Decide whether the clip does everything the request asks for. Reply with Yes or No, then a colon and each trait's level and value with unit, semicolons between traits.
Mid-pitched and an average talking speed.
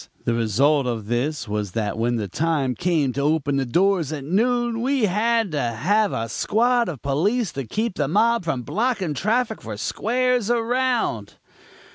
Yes: medium, 165 Hz; average, 170 wpm